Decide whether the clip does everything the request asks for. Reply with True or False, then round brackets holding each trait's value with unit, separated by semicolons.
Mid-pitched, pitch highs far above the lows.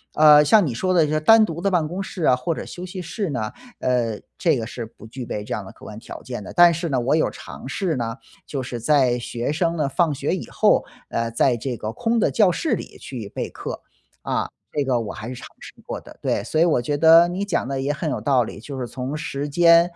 True (145 Hz; 5.7 semitones)